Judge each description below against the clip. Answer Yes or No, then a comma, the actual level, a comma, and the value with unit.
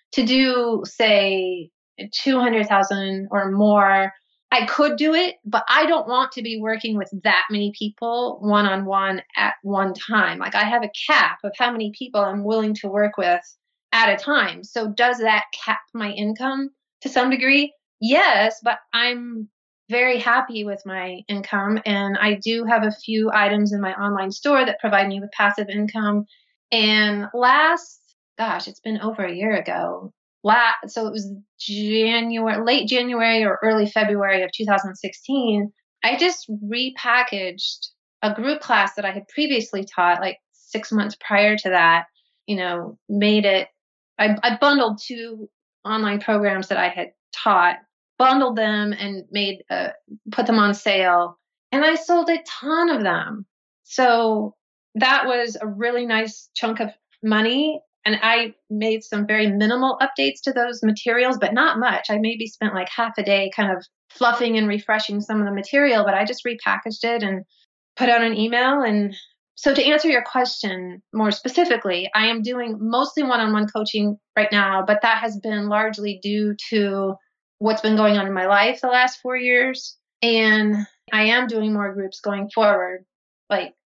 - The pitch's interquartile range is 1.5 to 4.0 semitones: Yes, average, 3.0 semitones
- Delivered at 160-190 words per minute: Yes, average, 170 wpm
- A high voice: Yes, high, 215 Hz